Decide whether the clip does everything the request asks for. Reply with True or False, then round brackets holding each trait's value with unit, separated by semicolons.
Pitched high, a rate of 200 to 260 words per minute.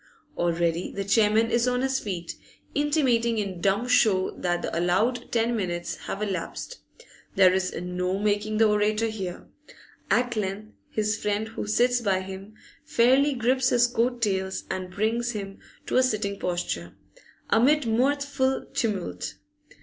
False (215 Hz; 145 wpm)